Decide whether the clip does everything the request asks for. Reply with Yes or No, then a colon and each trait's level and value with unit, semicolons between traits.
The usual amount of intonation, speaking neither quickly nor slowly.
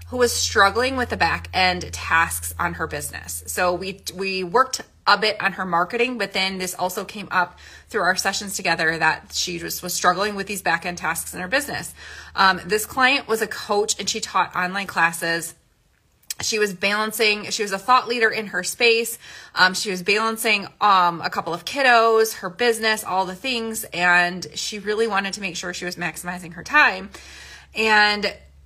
Yes: average, 3.6 semitones; average, 195 wpm